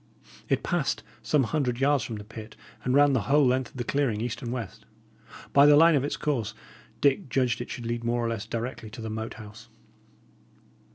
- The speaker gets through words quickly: Yes, fast, 210 wpm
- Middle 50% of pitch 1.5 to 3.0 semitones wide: No, average, 3.5 semitones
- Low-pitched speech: Yes, low, 120 Hz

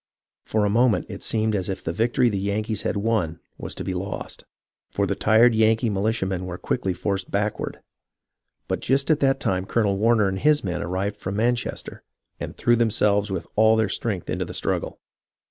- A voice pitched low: Yes, low, 105 Hz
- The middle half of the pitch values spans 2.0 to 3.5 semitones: Yes, average, 3.0 semitones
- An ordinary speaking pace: Yes, average, 190 wpm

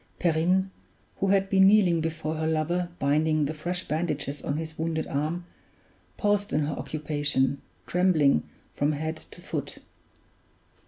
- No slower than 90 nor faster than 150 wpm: Yes, average, 140 wpm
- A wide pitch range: No, average, 2.9 semitones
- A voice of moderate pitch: Yes, medium, 160 Hz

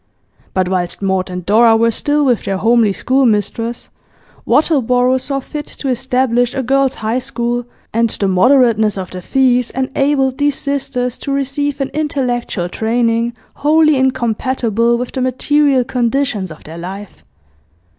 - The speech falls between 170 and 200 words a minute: No, average, 145 wpm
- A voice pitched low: No, high, 245 Hz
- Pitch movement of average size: Yes, average, 3.4 semitones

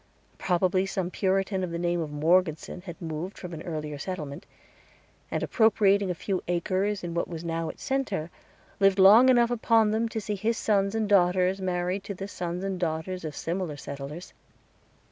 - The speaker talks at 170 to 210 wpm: Yes, average, 180 wpm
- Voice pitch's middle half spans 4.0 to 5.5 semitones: No, average, 2.9 semitones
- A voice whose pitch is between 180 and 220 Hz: Yes, medium, 185 Hz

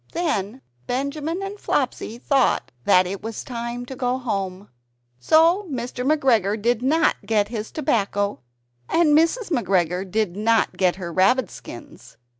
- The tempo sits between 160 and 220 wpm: No, average, 140 wpm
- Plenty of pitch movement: Yes, wide, 6.1 semitones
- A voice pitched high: Yes, high, 235 Hz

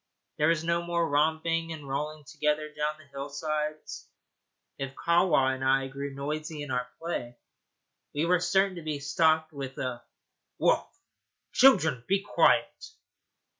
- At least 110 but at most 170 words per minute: Yes, average, 140 wpm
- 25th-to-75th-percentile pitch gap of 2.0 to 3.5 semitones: Yes, average, 2.9 semitones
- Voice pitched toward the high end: No, medium, 155 Hz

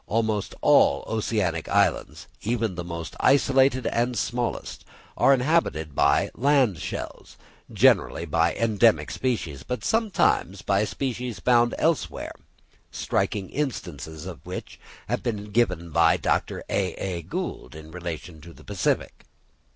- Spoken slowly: Yes, slow, 125 wpm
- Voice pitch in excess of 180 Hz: No, low, 105 Hz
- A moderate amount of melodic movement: No, wide, 6.4 semitones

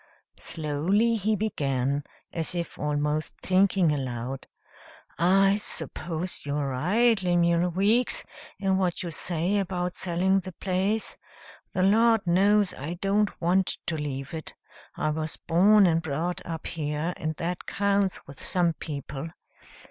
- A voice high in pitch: No, medium, 175 Hz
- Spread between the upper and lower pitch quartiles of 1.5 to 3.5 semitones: No, average, 4.0 semitones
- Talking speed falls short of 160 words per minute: Yes, slow, 135 wpm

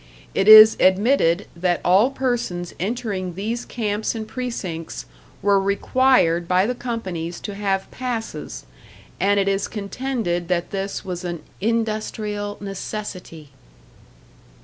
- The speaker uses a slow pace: Yes, slow, 120 wpm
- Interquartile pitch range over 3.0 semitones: Yes, average, 3.8 semitones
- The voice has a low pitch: No, high, 200 Hz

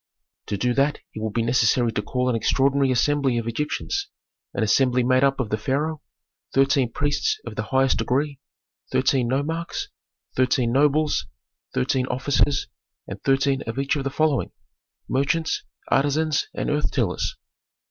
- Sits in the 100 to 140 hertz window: Yes, low, 135 Hz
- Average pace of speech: Yes, average, 150 wpm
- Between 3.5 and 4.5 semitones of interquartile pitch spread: No, average, 2.9 semitones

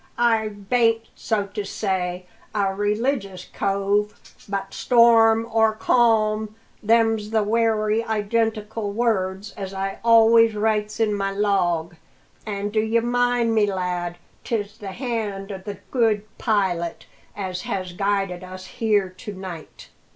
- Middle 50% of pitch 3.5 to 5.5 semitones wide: No, narrow, 2.4 semitones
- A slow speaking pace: Yes, slow, 130 wpm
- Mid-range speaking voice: No, high, 210 Hz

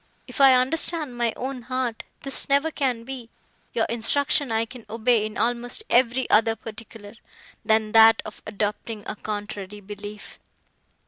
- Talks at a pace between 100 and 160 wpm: Yes, average, 145 wpm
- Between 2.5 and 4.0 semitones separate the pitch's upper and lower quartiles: Yes, average, 3.0 semitones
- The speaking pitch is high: Yes, high, 230 Hz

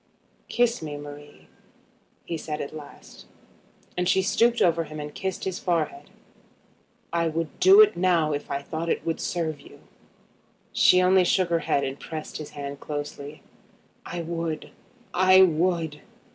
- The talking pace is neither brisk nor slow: Yes, average, 155 wpm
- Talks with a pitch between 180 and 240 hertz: No, medium, 165 Hz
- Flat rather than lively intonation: No, average, 3.4 semitones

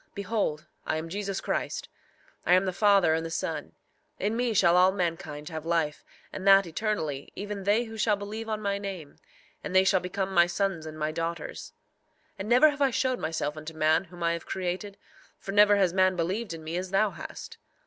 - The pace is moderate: No, fast, 210 wpm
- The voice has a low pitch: No, high, 190 Hz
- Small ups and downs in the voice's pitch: No, average, 3.7 semitones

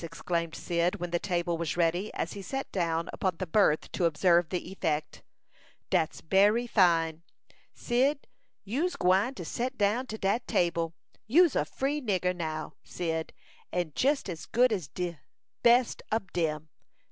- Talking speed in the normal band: Yes, average, 160 wpm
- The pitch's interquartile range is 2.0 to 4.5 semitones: No, average, 4.9 semitones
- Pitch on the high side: No, medium, 180 Hz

